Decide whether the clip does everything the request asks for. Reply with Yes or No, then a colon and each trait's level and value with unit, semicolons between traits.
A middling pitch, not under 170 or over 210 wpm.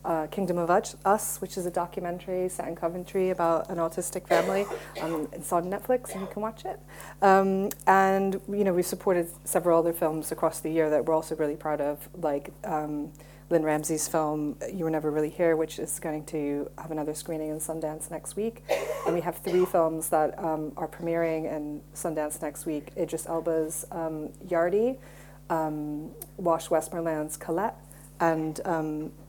Yes: medium, 165 Hz; average, 180 wpm